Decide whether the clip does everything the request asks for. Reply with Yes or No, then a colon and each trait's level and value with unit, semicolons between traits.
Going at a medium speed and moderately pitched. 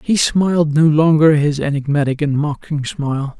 Yes: average, 160 wpm; medium, 150 Hz